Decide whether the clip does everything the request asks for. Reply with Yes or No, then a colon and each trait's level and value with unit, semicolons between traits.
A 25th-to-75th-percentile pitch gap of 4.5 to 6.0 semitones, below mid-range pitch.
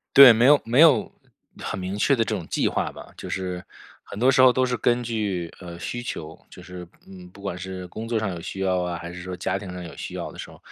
Yes: average, 4.9 semitones; very low, 95 Hz